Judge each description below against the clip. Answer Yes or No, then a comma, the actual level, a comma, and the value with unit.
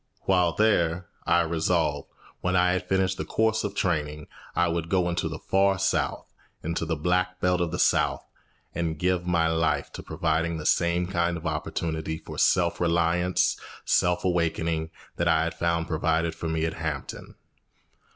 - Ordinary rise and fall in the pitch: No, narrow, 1.9 semitones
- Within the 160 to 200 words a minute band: Yes, average, 170 wpm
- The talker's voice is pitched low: Yes, very low, 85 Hz